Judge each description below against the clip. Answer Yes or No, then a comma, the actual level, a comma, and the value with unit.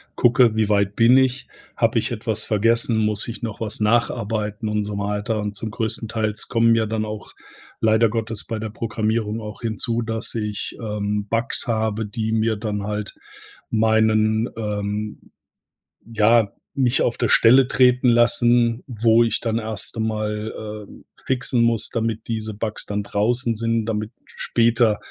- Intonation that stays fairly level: Yes, narrow, 1.5 semitones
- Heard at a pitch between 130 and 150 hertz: No, low, 110 Hz